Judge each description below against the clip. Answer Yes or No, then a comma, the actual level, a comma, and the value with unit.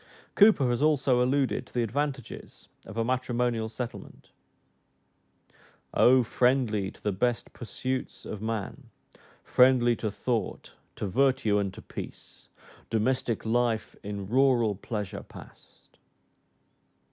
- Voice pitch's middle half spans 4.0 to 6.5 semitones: No, average, 3.0 semitones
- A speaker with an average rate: No, slow, 115 wpm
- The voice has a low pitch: Yes, low, 120 Hz